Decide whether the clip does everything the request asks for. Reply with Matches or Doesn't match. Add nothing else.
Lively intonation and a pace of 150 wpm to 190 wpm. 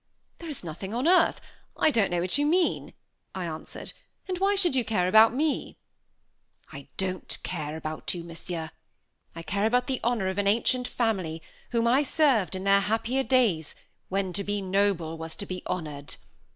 Matches